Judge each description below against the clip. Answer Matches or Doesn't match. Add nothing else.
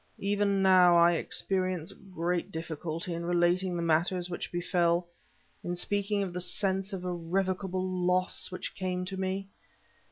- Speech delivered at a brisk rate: Doesn't match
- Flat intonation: Matches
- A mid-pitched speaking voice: Matches